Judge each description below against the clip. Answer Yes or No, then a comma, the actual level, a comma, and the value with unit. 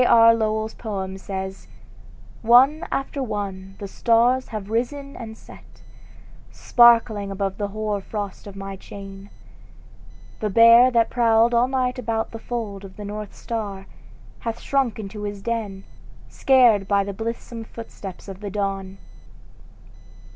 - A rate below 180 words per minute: Yes, average, 140 wpm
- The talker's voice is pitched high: Yes, high, 215 Hz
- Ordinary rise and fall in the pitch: Yes, average, 3.0 semitones